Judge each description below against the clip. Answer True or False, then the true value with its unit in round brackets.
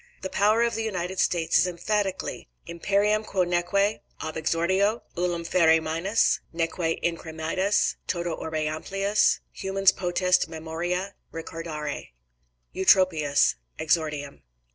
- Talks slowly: True (120 wpm)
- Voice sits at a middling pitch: True (175 Hz)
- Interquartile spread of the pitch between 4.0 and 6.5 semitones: False (3.3 semitones)